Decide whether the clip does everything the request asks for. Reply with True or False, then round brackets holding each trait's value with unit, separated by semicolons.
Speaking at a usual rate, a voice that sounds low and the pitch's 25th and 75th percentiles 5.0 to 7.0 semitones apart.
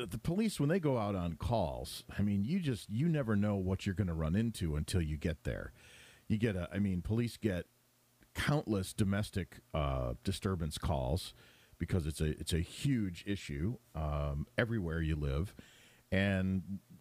True (175 wpm; 100 Hz; 5.6 semitones)